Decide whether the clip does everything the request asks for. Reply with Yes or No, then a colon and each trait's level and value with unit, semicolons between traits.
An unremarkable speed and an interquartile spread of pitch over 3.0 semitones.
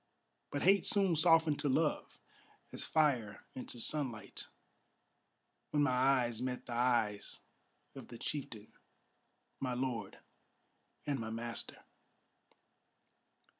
No: slow, 105 wpm; average, 3.9 semitones